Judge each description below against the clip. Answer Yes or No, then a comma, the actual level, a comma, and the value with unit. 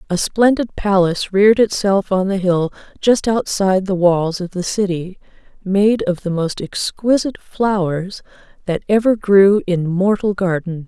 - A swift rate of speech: No, average, 150 wpm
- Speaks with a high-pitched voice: Yes, high, 195 Hz